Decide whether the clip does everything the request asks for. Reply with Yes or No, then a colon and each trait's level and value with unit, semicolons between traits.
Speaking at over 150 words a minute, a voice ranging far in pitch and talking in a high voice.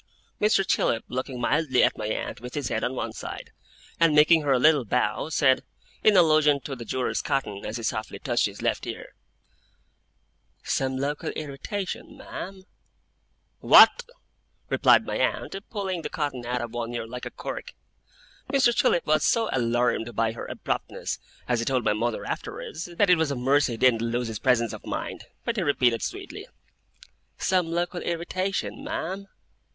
No: average, 170 wpm; wide, 5.8 semitones; low, 135 Hz